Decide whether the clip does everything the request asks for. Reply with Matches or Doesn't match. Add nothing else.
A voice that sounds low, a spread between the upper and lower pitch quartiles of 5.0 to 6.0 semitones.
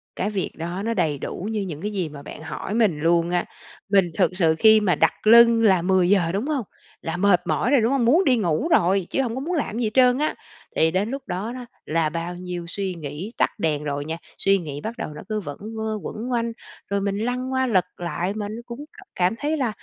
Doesn't match